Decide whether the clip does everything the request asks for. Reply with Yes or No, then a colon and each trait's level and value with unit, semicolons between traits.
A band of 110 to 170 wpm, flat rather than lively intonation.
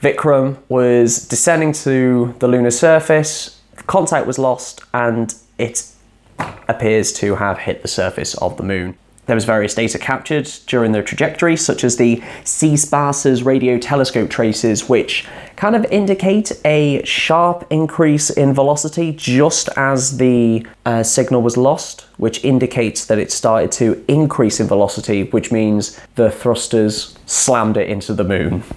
No: average, 150 wpm; average, 4.7 semitones